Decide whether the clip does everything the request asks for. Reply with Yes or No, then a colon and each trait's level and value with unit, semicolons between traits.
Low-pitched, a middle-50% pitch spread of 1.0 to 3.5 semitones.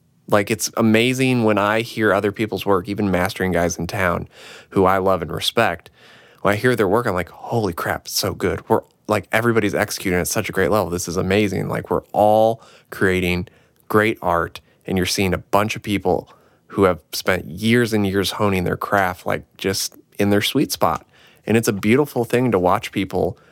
Yes: low, 100 Hz; average, 3.0 semitones